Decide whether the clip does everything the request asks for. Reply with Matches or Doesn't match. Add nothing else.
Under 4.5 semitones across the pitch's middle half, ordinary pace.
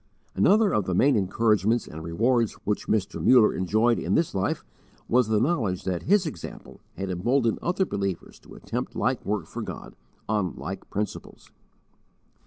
Doesn't match